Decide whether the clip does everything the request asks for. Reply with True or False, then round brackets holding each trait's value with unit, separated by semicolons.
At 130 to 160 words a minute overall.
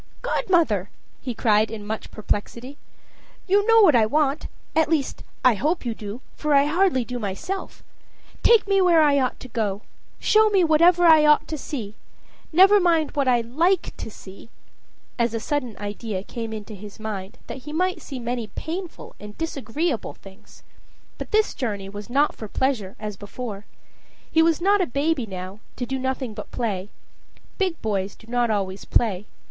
False (175 wpm)